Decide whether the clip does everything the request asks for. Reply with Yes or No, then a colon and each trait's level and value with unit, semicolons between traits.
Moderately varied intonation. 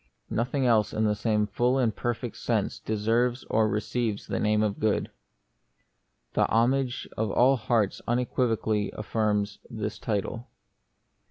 No: narrow, 2.3 semitones